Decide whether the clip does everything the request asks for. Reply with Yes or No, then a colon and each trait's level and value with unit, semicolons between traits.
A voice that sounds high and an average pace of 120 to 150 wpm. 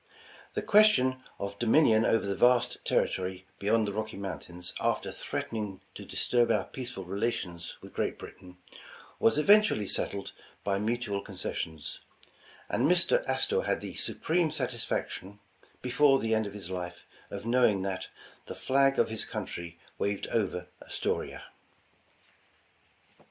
No: low, 110 Hz; slow, 135 wpm